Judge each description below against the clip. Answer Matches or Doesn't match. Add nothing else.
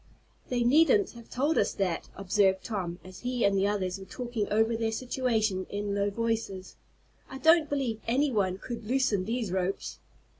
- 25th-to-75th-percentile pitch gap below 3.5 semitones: Doesn't match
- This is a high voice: Matches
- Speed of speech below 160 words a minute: Doesn't match